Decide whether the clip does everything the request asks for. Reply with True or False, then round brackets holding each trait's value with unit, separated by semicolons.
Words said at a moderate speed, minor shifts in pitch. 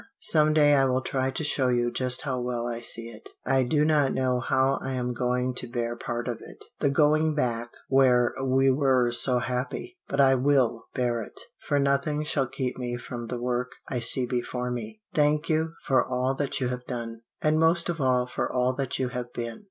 False (215 wpm; 2.2 semitones)